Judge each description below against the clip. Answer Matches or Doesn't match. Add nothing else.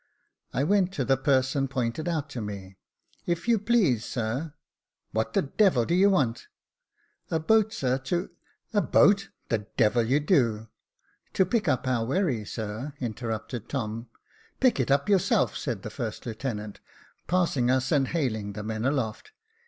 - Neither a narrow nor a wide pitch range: Doesn't match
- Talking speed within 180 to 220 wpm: Matches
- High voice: Doesn't match